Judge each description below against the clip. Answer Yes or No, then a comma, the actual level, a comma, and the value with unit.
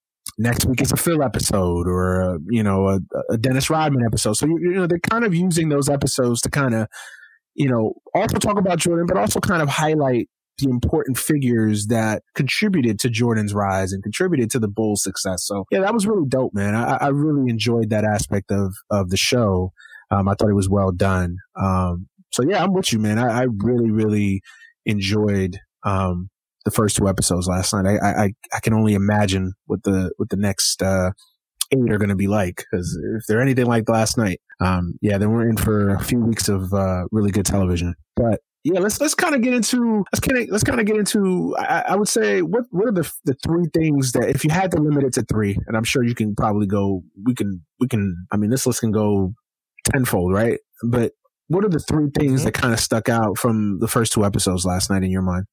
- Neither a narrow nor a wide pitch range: No, wide, 6.3 semitones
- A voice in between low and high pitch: No, low, 110 Hz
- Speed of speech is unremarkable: No, fast, 230 wpm